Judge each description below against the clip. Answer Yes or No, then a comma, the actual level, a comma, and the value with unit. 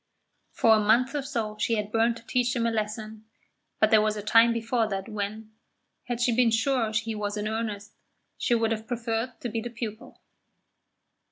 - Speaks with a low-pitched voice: No, high, 225 Hz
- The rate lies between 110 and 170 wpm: No, average, 195 wpm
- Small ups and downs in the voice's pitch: Yes, narrow, 1.6 semitones